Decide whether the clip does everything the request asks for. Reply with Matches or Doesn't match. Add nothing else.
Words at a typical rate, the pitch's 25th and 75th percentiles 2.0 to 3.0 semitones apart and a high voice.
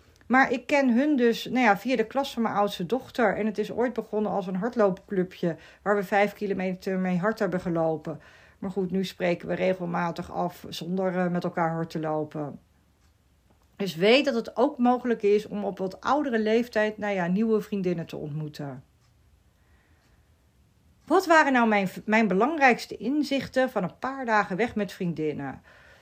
Doesn't match